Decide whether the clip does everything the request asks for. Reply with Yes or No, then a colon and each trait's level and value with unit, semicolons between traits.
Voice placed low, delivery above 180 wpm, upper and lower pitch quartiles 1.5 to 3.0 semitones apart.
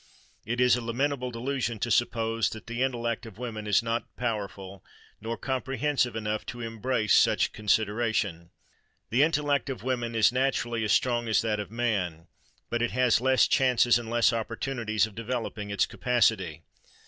No: low, 115 Hz; average, 160 wpm; narrow, 2.5 semitones